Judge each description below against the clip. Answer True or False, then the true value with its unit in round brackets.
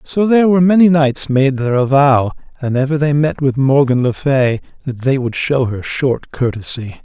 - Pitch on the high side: False (140 Hz)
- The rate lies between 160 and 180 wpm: False (195 wpm)